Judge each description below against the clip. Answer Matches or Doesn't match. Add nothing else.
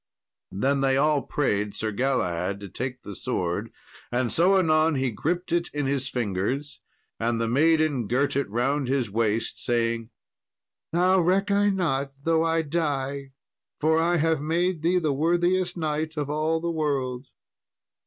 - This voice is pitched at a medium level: Matches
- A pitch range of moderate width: Matches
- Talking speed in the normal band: Matches